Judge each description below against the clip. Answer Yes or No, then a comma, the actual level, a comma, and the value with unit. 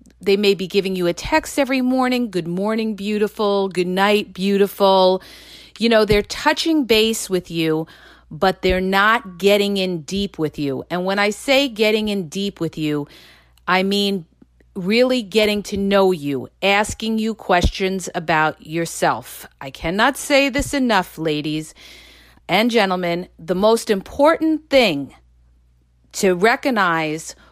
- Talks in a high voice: Yes, high, 195 Hz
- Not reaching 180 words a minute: Yes, average, 140 wpm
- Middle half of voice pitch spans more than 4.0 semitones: Yes, average, 4.4 semitones